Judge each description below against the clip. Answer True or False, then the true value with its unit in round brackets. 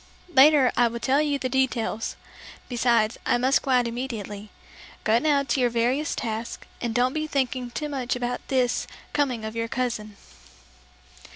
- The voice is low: False (245 Hz)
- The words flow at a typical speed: True (165 wpm)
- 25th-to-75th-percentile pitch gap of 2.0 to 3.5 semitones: True (2.5 semitones)